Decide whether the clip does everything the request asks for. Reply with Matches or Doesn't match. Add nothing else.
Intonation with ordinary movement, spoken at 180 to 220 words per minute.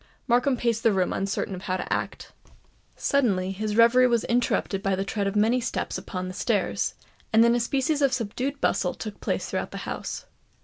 Matches